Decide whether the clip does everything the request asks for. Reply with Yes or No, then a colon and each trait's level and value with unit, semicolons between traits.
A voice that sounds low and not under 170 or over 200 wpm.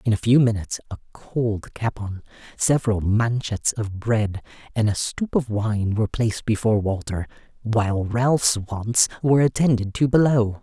No: low, 115 Hz; average, 150 wpm